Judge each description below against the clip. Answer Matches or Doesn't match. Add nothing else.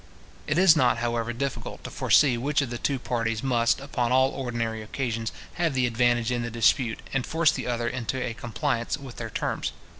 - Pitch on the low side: Matches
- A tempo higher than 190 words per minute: Matches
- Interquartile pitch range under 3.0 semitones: Matches